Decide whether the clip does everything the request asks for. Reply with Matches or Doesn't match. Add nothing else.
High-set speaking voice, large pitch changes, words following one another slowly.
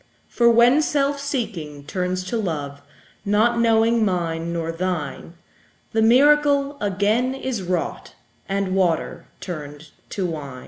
Matches